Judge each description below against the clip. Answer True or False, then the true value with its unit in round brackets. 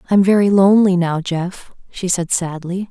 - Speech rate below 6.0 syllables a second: True (5.1 syllables/s)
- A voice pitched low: False (185 Hz)